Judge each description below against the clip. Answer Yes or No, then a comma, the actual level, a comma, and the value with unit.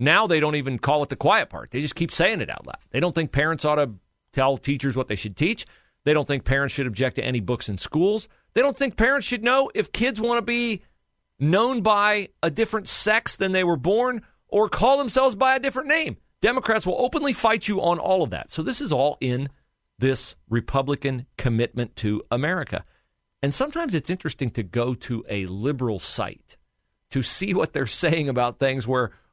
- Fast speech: Yes, fast, 210 wpm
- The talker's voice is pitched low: No, medium, 150 Hz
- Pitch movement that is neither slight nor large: No, wide, 8.8 semitones